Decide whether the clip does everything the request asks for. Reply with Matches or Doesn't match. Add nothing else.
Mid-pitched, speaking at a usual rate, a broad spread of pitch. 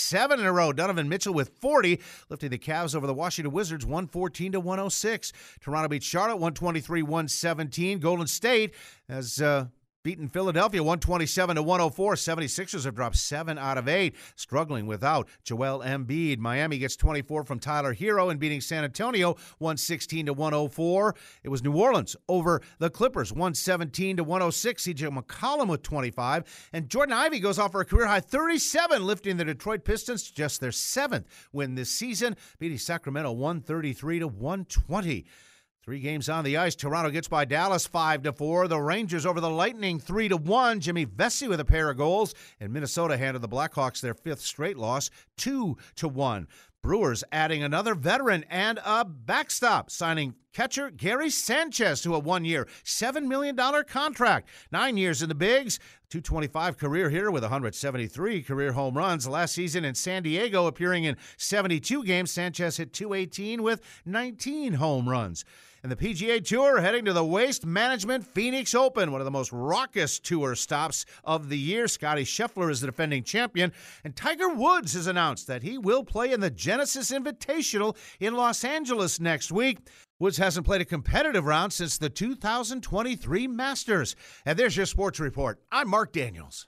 Matches